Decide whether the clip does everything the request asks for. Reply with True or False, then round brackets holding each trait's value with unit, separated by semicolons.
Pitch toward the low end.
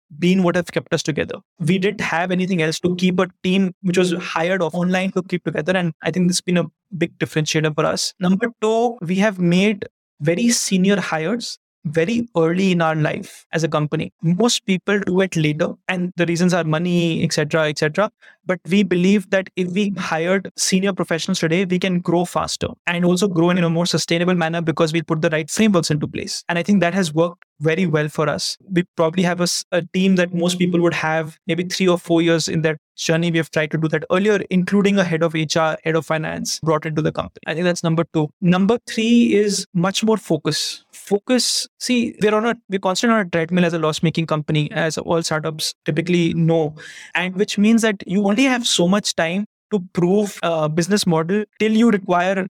False (175 Hz)